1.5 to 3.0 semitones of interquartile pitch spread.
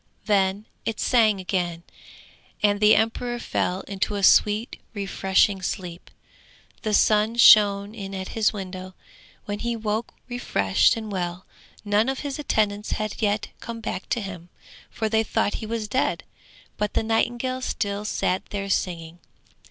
Yes: narrow, 2.6 semitones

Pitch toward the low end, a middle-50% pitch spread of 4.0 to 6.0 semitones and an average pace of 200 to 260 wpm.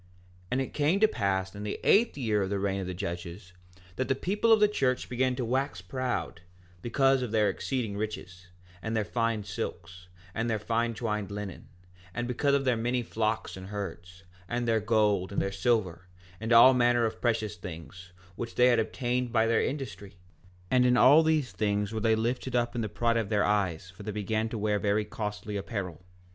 No: low, 110 Hz; average, 3.6 semitones; fast, 205 wpm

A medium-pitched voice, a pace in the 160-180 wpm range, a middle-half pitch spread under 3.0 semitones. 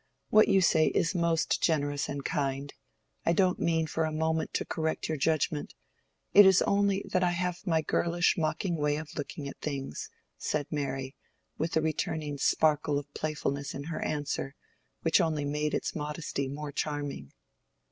Yes: medium, 155 Hz; average, 165 wpm; narrow, 2.5 semitones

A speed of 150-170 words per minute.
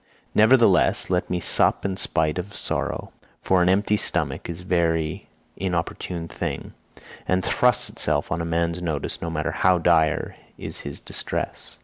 Yes: average, 155 wpm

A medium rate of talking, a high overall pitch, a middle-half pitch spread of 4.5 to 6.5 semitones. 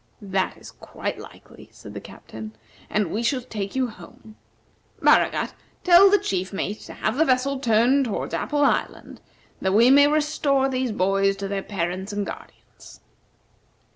Yes: average, 160 wpm; high, 220 Hz; wide, 5.6 semitones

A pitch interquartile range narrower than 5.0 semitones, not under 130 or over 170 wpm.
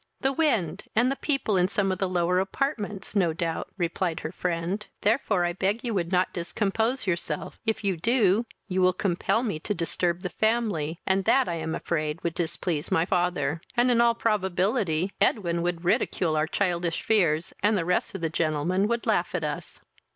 No: average, 3.8 semitones; average, 190 wpm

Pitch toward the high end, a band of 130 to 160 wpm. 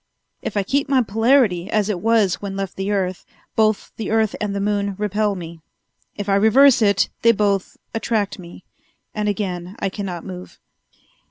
No: high, 205 Hz; average, 175 wpm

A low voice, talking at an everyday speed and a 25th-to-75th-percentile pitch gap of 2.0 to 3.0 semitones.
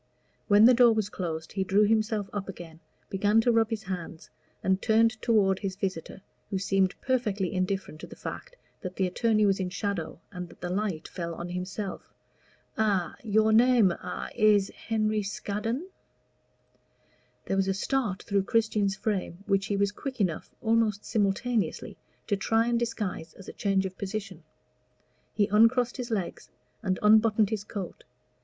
No: high, 205 Hz; average, 165 wpm; narrow, 2.6 semitones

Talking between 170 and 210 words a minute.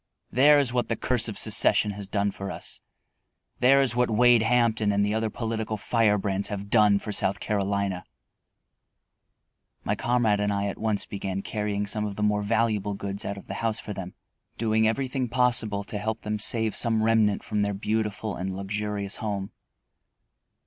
Yes: average, 175 wpm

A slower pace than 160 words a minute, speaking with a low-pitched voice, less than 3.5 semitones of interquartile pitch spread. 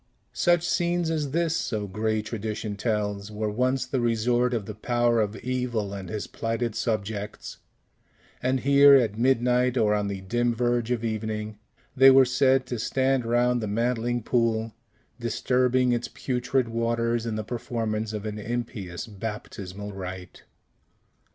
Yes: average, 150 wpm; low, 115 Hz; average, 2.7 semitones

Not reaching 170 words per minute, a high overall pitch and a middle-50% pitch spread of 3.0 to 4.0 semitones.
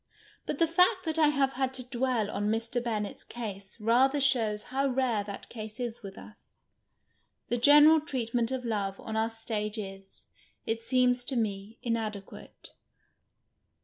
Yes: average, 155 wpm; high, 235 Hz; average, 3.7 semitones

